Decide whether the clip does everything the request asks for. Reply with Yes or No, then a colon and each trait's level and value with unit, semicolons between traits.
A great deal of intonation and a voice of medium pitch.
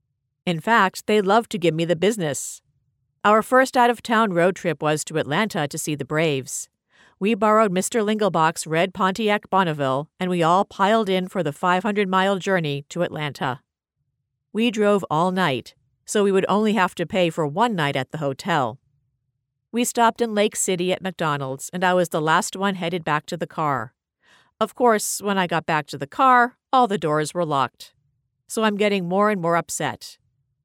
Yes: wide, 6.0 semitones; medium, 180 Hz